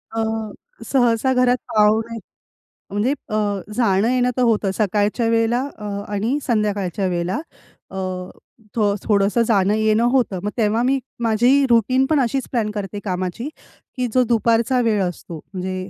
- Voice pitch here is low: No, high, 220 Hz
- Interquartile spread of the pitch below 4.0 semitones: Yes, average, 3.3 semitones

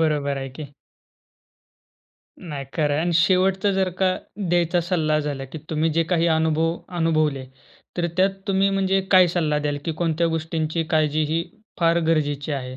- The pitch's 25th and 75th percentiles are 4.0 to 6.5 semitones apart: No, narrow, 2.5 semitones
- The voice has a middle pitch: Yes, medium, 160 Hz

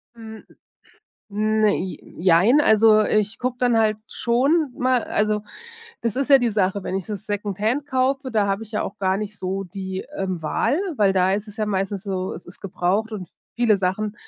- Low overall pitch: No, high, 210 Hz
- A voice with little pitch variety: No, average, 3.0 semitones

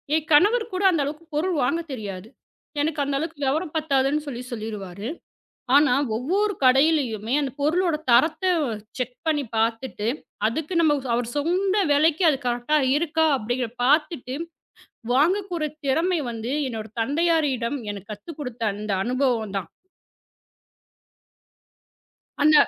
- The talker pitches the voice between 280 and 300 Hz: Yes, very high, 285 Hz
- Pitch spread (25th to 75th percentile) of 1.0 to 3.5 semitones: No, average, 5.2 semitones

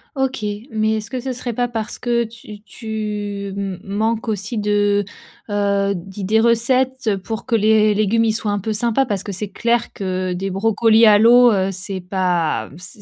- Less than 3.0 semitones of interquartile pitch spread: Yes, narrow, 2.5 semitones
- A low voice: No, high, 215 Hz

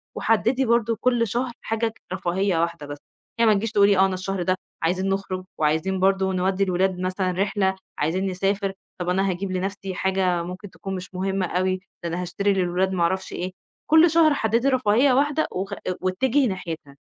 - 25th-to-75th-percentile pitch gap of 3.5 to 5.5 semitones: No, narrow, 2.4 semitones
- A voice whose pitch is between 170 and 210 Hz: Yes, high, 190 Hz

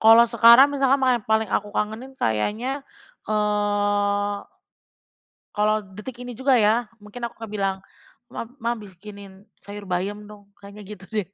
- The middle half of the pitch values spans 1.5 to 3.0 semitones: Yes, narrow, 2.5 semitones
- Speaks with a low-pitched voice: No, high, 210 Hz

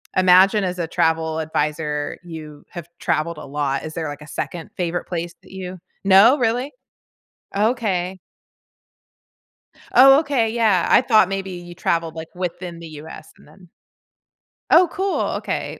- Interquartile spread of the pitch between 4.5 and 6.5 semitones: No, average, 3.8 semitones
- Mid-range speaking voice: Yes, medium, 180 Hz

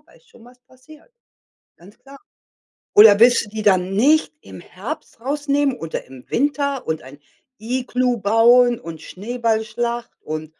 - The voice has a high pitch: Yes, high, 235 Hz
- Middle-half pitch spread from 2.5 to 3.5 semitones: No, average, 4.1 semitones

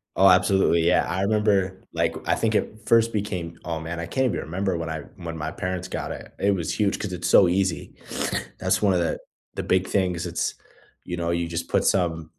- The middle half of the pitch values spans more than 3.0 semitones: No, narrow, 2.6 semitones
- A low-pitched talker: Yes, very low, 90 Hz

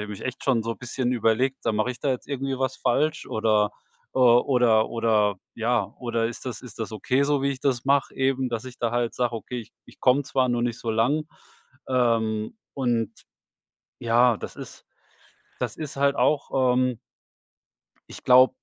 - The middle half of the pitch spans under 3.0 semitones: Yes, narrow, 2.6 semitones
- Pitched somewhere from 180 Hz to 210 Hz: No, low, 125 Hz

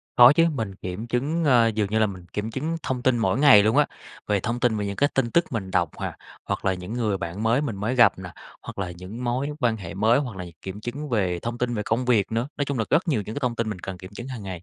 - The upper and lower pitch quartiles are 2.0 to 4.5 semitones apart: Yes, average, 4.2 semitones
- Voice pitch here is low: Yes, low, 115 Hz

